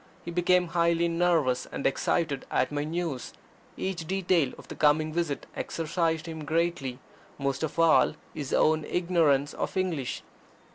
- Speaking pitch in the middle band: Yes, medium, 165 Hz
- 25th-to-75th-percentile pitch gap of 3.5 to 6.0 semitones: No, average, 2.8 semitones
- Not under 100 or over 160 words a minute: Yes, average, 145 wpm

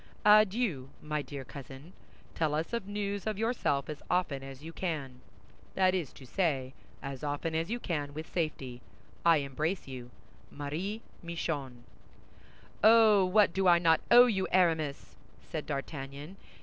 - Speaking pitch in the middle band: Yes, medium, 160 Hz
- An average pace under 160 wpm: Yes, average, 145 wpm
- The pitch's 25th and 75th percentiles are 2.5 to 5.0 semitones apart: No, wide, 5.4 semitones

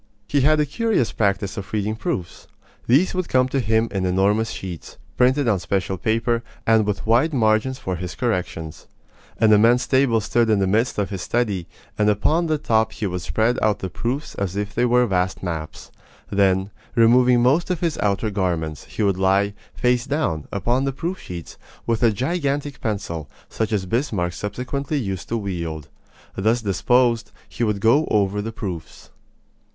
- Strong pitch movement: No, average, 4.5 semitones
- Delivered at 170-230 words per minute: Yes, average, 180 wpm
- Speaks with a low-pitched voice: Yes, low, 110 Hz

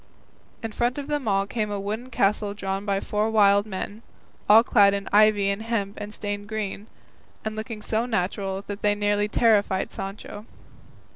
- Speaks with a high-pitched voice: Yes, high, 205 Hz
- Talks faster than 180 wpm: No, average, 165 wpm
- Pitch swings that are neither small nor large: No, narrow, 1.6 semitones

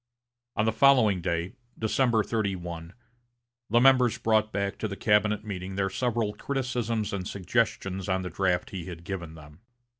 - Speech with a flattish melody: No, average, 3.6 semitones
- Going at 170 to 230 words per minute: No, average, 155 wpm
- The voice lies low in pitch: Yes, low, 100 Hz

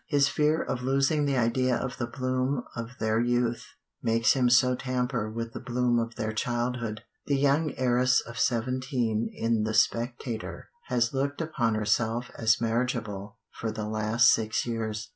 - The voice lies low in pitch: Yes, low, 120 Hz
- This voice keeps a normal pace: Yes, average, 160 wpm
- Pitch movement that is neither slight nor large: No, narrow, 2.2 semitones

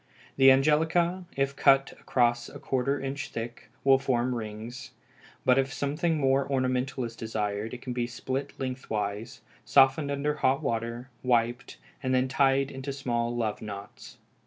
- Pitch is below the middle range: Yes, low, 130 Hz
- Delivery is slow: No, average, 145 wpm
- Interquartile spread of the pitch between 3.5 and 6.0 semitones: No, narrow, 2.5 semitones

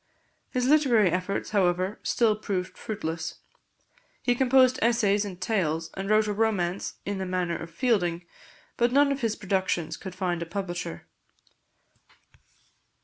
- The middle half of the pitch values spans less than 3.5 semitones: No, average, 4.3 semitones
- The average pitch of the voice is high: Yes, high, 195 Hz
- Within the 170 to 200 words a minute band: No, average, 140 wpm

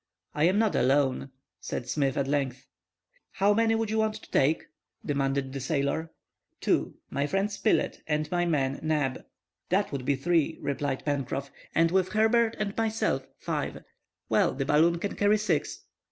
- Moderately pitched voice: Yes, medium, 155 Hz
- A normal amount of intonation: No, wide, 6.7 semitones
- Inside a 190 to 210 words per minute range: No, average, 165 wpm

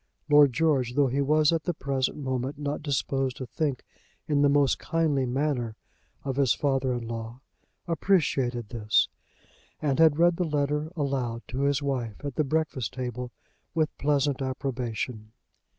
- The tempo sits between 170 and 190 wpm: No, average, 155 wpm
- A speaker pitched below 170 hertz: Yes, medium, 140 Hz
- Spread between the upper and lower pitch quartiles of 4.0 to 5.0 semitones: No, average, 2.9 semitones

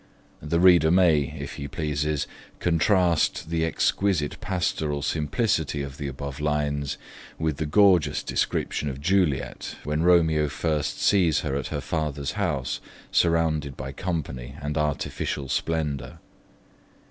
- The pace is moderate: No, slow, 125 wpm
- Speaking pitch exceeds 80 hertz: No, very low, 75 Hz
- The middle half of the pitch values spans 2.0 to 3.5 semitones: Yes, average, 2.8 semitones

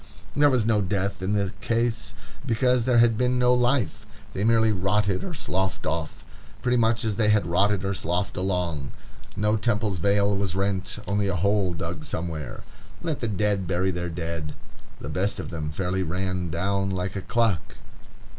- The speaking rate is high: No, average, 175 wpm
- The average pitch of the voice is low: Yes, low, 100 Hz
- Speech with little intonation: No, average, 3.7 semitones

